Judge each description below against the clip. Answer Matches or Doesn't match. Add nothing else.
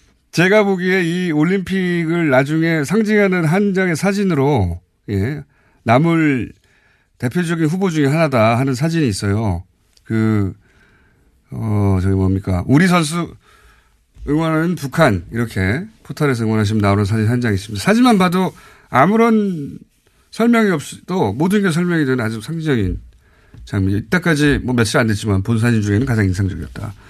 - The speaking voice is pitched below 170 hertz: Matches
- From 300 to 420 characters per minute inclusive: Matches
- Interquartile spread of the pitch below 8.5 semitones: Doesn't match